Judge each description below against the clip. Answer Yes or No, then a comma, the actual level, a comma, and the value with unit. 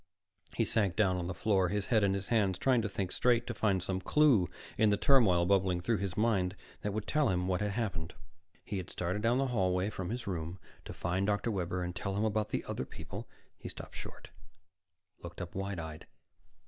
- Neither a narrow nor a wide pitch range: Yes, average, 3.1 semitones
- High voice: No, low, 100 Hz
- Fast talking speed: Yes, fast, 215 wpm